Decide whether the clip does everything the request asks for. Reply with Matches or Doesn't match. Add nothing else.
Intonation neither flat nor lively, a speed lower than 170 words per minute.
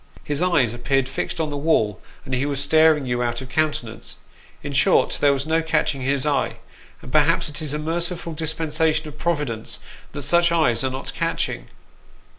Doesn't match